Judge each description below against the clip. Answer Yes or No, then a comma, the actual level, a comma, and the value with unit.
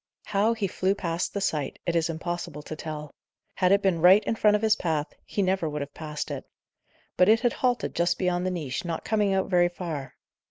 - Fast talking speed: Yes, fast, 225 wpm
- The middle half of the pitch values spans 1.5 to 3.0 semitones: No, average, 3.8 semitones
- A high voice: No, medium, 175 Hz